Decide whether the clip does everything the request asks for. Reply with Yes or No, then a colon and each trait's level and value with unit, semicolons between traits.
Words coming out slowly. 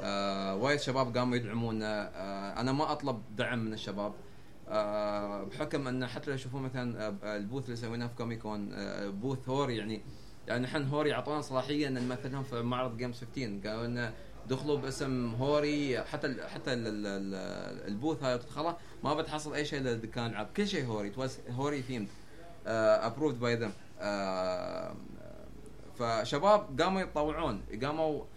No: fast, 135 wpm